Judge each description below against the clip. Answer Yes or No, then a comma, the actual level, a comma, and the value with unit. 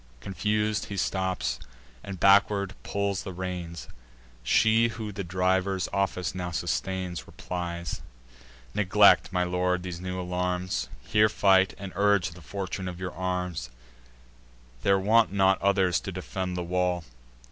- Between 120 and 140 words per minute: Yes, slow, 135 wpm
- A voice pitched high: No, very low, 95 Hz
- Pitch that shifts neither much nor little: No, narrow, 1.7 semitones